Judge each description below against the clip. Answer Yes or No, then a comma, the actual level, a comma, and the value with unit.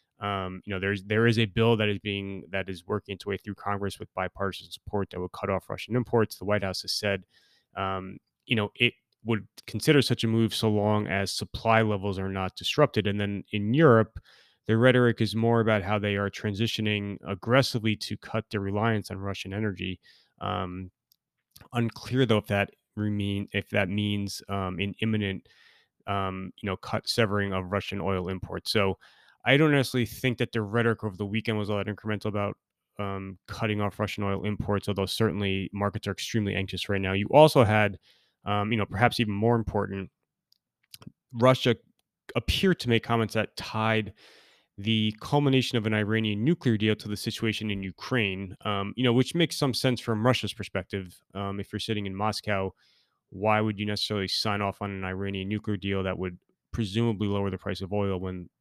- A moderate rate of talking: Yes, average, 190 wpm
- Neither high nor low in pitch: No, low, 105 Hz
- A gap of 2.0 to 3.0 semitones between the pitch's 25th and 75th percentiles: Yes, narrow, 2.4 semitones